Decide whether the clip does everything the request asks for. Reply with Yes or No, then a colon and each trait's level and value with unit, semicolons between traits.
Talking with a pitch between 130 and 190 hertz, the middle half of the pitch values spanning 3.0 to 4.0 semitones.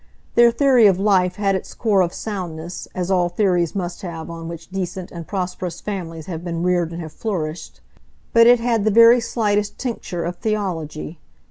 Yes: medium, 185 Hz; average, 3.6 semitones